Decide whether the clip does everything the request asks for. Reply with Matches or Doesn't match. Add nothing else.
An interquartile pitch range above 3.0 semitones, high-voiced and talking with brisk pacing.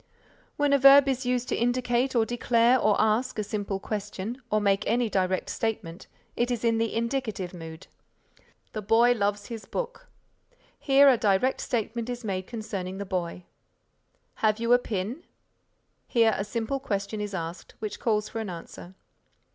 Doesn't match